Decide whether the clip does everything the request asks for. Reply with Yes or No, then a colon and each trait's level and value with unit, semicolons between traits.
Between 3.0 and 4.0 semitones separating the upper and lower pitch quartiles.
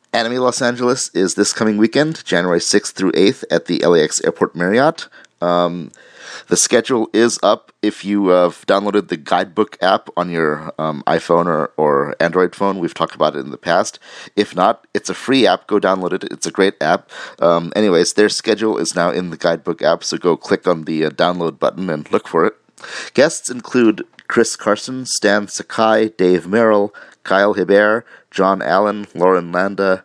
Yes: average, 3.7 semitones